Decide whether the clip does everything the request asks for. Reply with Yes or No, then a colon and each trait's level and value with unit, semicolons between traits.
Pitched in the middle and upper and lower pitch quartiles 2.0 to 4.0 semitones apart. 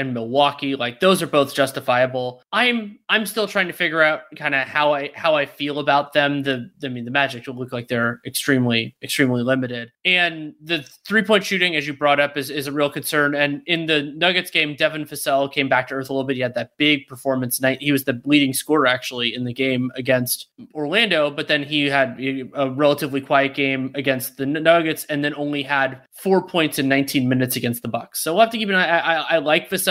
Yes: medium, 145 Hz; average, 2.8 semitones